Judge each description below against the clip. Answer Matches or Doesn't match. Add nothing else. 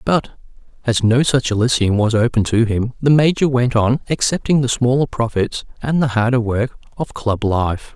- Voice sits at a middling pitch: Doesn't match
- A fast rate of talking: Doesn't match